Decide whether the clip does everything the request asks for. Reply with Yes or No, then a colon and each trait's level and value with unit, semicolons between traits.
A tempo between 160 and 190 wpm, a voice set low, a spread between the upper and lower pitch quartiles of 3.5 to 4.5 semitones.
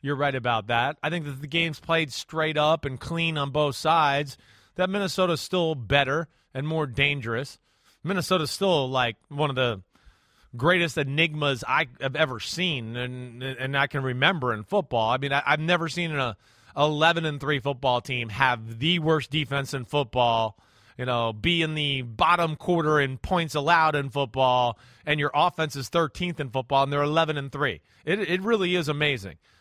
No: average, 180 wpm; medium, 145 Hz; average, 3.9 semitones